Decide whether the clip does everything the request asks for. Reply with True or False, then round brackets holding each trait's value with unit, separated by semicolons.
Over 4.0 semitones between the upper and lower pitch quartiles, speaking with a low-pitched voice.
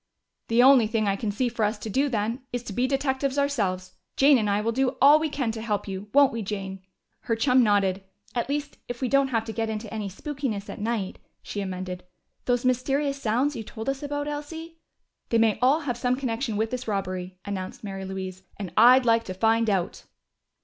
False (4.6 semitones; 230 Hz)